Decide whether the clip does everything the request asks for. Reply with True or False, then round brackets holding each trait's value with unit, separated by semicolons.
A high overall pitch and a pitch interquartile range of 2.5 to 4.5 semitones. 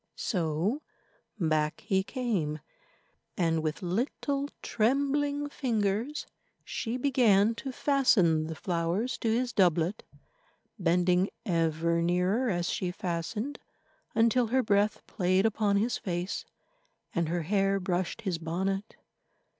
False (195 Hz; 5.3 semitones)